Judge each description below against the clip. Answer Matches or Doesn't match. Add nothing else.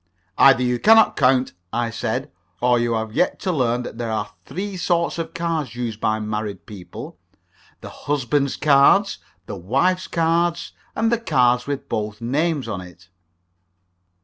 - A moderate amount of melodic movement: Doesn't match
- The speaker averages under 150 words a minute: Doesn't match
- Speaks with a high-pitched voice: Doesn't match